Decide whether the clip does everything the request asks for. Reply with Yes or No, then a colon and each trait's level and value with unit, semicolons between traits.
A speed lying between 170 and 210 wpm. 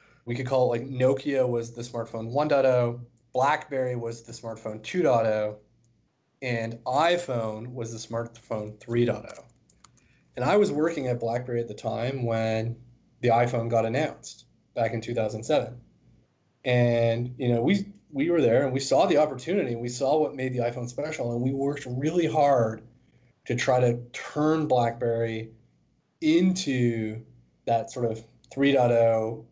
No: average, 150 wpm